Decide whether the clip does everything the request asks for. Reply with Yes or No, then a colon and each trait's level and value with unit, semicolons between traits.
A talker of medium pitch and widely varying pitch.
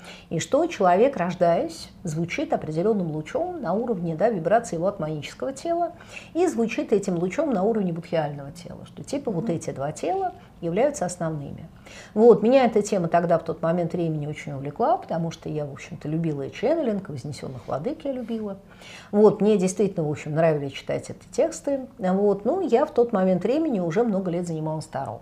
Yes: medium, 180 Hz; wide, 5.9 semitones